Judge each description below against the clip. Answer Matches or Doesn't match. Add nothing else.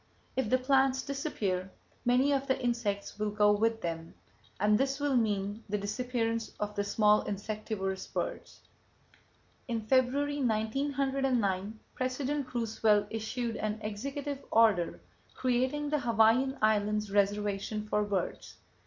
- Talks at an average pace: Doesn't match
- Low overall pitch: Doesn't match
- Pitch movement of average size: Matches